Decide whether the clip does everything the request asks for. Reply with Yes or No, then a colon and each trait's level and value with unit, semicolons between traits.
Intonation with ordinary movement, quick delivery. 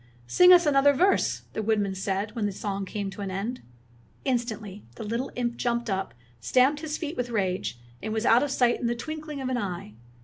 Yes: average, 4.9 semitones; fast, 210 wpm